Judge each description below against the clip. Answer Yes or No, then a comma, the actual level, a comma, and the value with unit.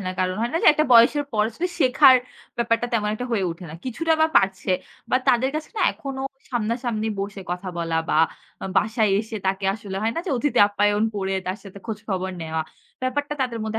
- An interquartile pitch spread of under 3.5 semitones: No, average, 4.3 semitones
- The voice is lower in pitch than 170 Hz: No, high, 220 Hz